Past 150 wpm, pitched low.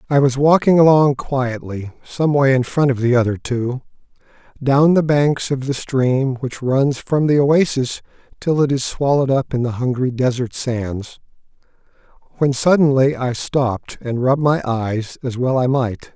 Yes: average, 170 wpm; low, 130 Hz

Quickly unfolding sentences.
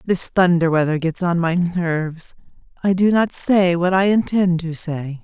No: average, 185 wpm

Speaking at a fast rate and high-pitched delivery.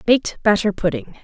No: average, 145 wpm; high, 200 Hz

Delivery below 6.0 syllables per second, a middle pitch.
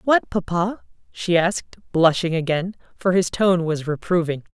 Yes: 4.5 syllables/s; medium, 175 Hz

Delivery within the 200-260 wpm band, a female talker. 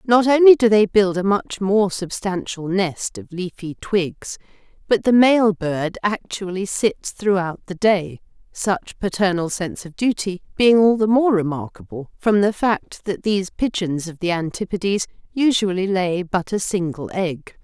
No: average, 160 wpm; female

